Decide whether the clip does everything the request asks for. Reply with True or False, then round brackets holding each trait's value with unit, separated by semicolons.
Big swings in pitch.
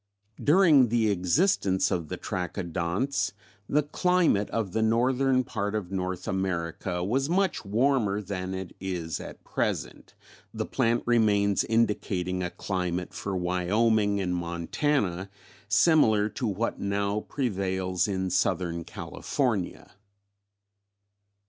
False (4.3 semitones)